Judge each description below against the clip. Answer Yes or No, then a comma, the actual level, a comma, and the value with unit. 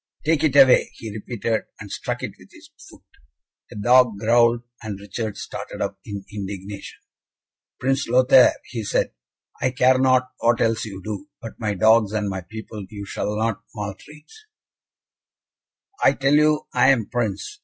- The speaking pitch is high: No, low, 115 Hz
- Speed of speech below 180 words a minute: Yes, average, 160 wpm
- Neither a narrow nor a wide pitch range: Yes, average, 3.8 semitones